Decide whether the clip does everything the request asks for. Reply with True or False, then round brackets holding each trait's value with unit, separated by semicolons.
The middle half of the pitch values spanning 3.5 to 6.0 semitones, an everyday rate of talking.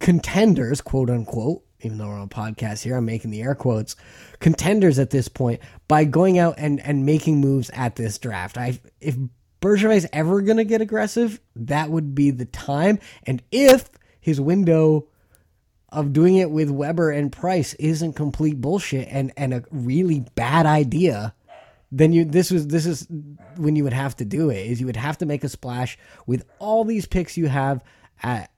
True (5.1 semitones; 190 wpm)